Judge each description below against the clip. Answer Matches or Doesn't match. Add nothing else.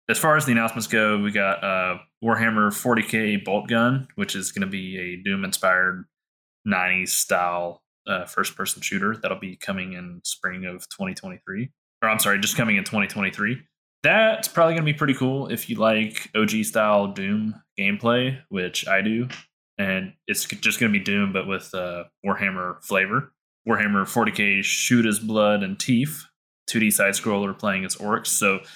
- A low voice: Matches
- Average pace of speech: Matches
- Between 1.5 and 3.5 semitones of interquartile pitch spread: Doesn't match